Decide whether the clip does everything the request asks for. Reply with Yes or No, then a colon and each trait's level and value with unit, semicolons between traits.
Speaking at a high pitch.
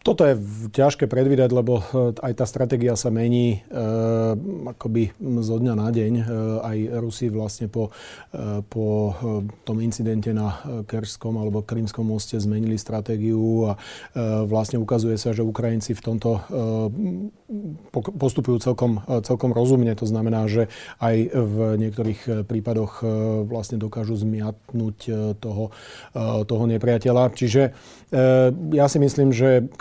No: low, 115 Hz